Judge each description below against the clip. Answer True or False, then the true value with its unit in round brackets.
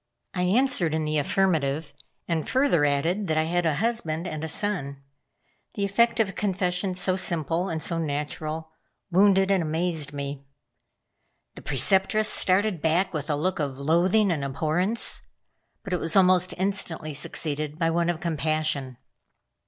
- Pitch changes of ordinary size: True (3.8 semitones)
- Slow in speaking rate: False (155 wpm)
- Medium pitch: True (165 Hz)